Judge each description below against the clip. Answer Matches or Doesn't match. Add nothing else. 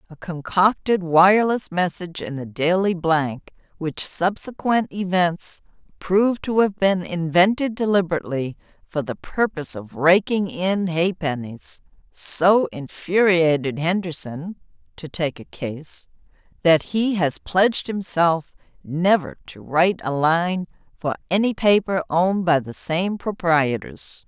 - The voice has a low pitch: Doesn't match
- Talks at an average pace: Doesn't match